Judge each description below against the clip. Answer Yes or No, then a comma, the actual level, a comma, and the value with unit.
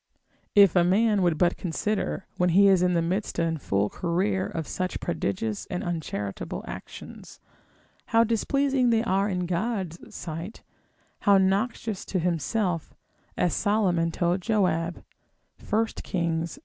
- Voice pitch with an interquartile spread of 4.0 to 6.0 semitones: No, average, 3.5 semitones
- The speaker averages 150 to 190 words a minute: No, average, 140 wpm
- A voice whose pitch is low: No, medium, 180 Hz